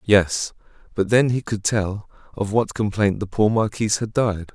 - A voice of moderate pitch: No, low, 105 Hz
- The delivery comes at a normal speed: Yes, average, 185 wpm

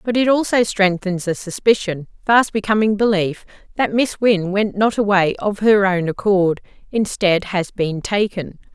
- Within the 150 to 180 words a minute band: Yes, average, 160 wpm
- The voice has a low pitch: No, high, 200 Hz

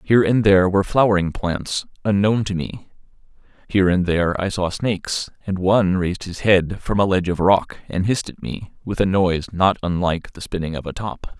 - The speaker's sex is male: Yes, male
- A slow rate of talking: No, fast, 205 wpm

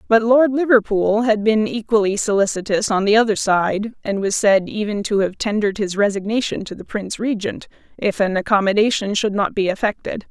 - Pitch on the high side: Yes, high, 210 Hz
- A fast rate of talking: No, average, 180 wpm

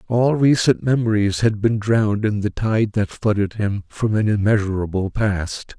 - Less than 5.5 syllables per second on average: Yes, 4.5 syllables/s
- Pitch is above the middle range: No, low, 105 Hz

